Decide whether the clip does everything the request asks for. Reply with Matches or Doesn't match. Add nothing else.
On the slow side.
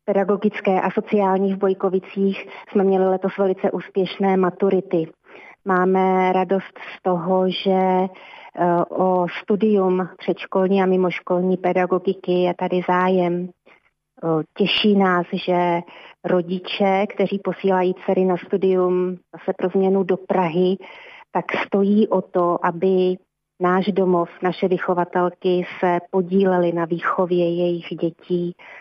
Matches